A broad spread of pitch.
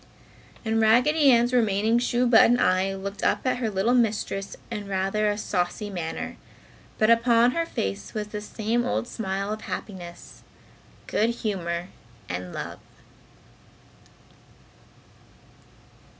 No: average, 3.5 semitones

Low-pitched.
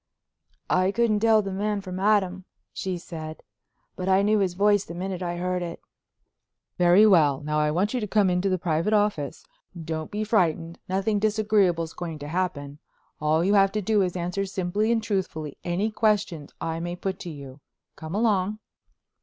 No: medium, 185 Hz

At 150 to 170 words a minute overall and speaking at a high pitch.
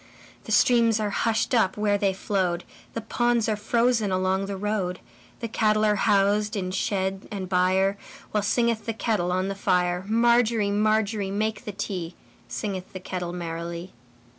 No: average, 140 wpm; high, 200 Hz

